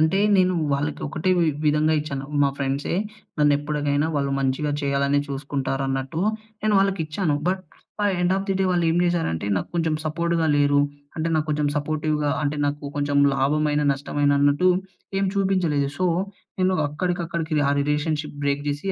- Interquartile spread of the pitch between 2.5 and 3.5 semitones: Yes, average, 2.8 semitones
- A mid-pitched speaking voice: Yes, medium, 150 Hz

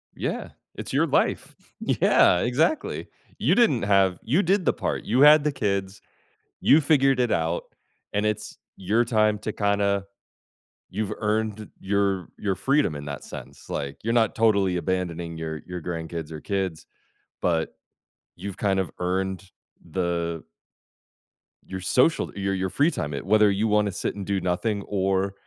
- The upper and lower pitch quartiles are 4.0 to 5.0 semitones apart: No, average, 3.4 semitones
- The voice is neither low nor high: No, low, 100 Hz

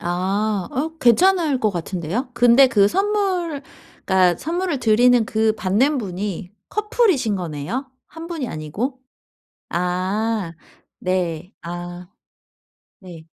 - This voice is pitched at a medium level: No, high, 220 Hz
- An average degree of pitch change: No, wide, 7.5 semitones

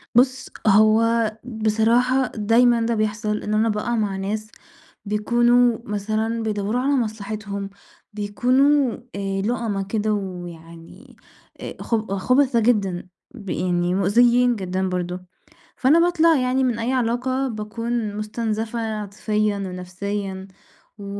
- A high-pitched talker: Yes, high, 215 Hz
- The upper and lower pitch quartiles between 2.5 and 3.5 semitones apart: Yes, average, 3.1 semitones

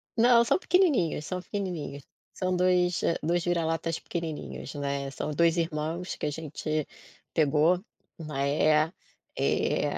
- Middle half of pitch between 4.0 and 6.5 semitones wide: No, average, 3.1 semitones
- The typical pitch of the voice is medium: Yes, medium, 165 Hz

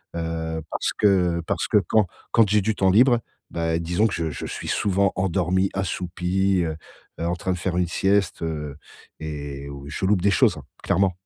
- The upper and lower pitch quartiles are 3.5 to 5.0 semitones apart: No, average, 3.0 semitones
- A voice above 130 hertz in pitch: No, very low, 90 Hz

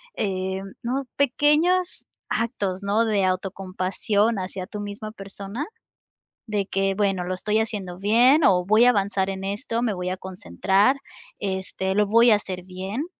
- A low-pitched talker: No, high, 200 Hz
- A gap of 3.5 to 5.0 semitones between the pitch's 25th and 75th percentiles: No, average, 2.9 semitones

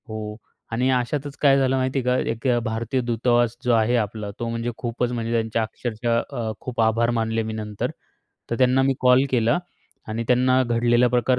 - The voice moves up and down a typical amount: No, narrow, 2.0 semitones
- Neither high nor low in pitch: No, low, 120 Hz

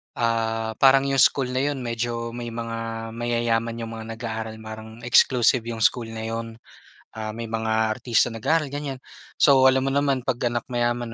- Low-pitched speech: Yes, low, 115 Hz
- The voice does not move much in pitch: Yes, narrow, 2.0 semitones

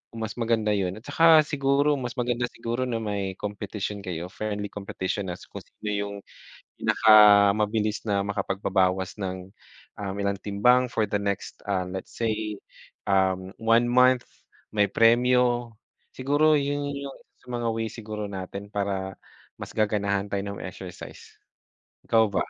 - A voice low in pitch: Yes, low, 105 Hz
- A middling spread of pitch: Yes, average, 3.2 semitones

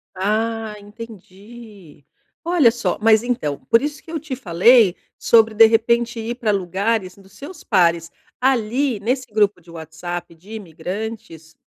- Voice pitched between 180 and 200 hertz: No, high, 220 Hz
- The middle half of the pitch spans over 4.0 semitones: Yes, average, 4.4 semitones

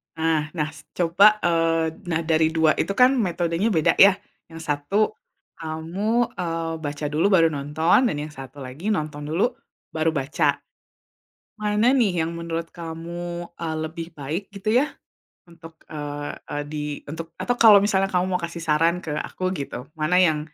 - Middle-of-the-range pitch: Yes, medium, 165 Hz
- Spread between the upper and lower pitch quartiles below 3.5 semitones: Yes, average, 2.8 semitones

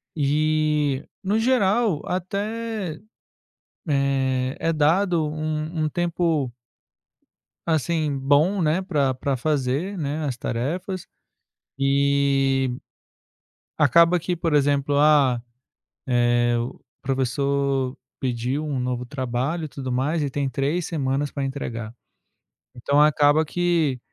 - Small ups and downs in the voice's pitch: No, average, 3.6 semitones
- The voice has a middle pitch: Yes, medium, 145 Hz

